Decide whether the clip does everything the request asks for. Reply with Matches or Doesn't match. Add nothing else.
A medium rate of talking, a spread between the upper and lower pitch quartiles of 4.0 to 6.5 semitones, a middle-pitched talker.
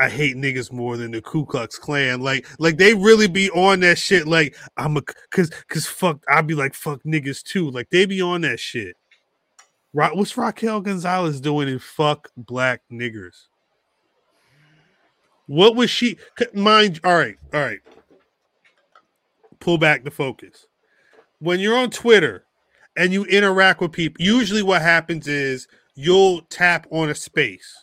Matches